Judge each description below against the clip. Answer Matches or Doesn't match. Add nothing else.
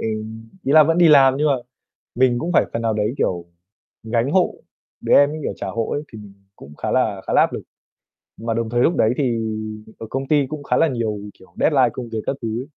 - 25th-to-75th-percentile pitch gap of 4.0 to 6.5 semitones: Matches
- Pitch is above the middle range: Doesn't match